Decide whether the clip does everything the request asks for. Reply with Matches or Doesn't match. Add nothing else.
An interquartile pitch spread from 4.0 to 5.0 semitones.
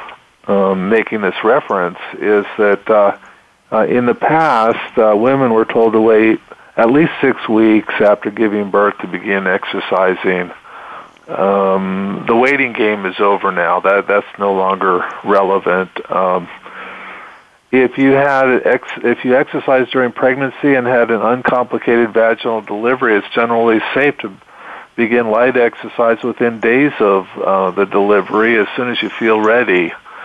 Doesn't match